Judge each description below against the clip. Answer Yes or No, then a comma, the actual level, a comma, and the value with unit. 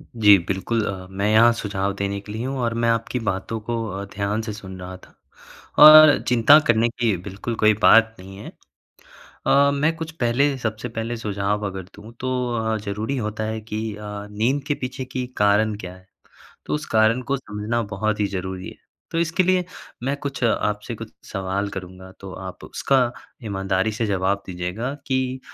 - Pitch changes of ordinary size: Yes, average, 3.6 semitones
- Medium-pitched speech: No, low, 110 Hz